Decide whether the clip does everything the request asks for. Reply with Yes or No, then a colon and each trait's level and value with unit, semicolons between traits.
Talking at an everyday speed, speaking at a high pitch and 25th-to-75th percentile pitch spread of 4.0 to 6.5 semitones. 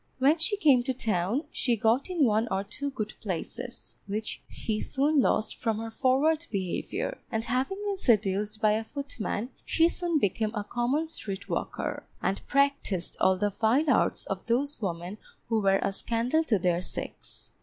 Yes: average, 175 wpm; high, 230 Hz; average, 5.2 semitones